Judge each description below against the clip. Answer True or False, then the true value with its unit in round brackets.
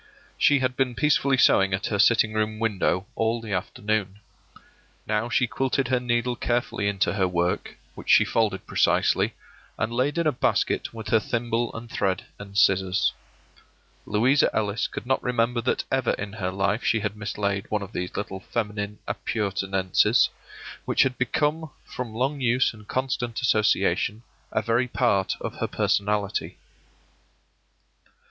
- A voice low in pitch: True (110 Hz)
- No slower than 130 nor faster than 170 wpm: True (155 wpm)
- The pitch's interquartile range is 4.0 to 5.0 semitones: False (3.4 semitones)